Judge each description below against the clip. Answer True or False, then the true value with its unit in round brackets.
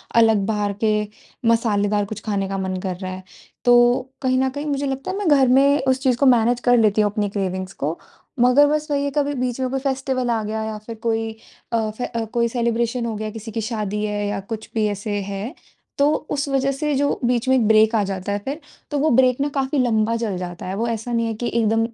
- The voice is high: True (230 Hz)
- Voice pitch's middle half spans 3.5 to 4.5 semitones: True (3.8 semitones)